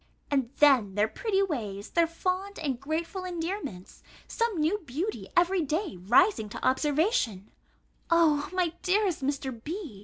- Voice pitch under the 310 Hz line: No, very high, 315 Hz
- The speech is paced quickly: No, average, 140 wpm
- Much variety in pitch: Yes, wide, 6.2 semitones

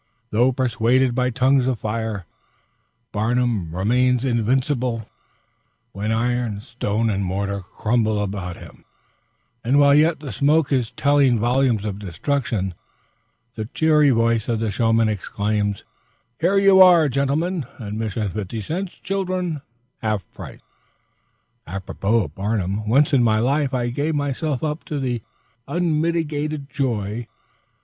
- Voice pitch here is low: Yes, low, 120 Hz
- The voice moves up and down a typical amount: Yes, average, 5.0 semitones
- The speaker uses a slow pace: Yes, slow, 125 wpm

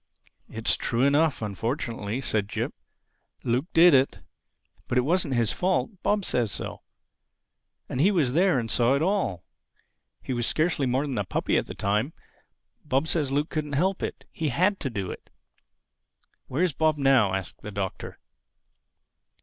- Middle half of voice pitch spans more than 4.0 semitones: Yes, wide, 5.5 semitones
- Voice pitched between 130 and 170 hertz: Yes, low, 135 Hz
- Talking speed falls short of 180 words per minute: Yes, average, 160 wpm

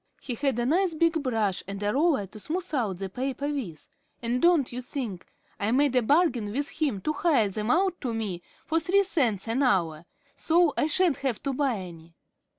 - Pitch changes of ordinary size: No, wide, 6.7 semitones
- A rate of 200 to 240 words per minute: Yes, fast, 205 wpm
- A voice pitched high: Yes, very high, 255 Hz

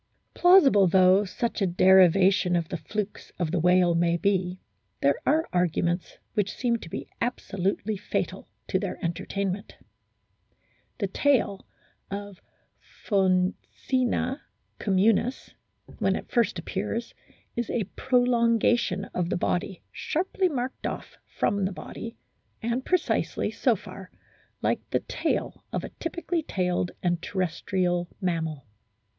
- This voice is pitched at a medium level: No, high, 195 Hz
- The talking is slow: Yes, slow, 125 wpm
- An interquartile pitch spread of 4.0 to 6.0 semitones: Yes, average, 4.6 semitones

